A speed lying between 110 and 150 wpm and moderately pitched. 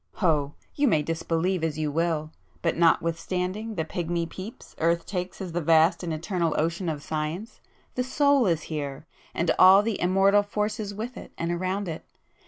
No: average, 170 wpm; medium, 170 Hz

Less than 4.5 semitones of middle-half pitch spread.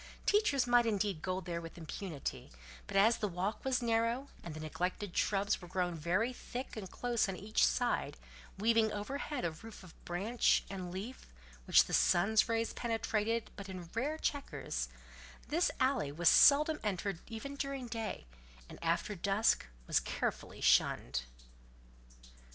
No: average, 5.1 semitones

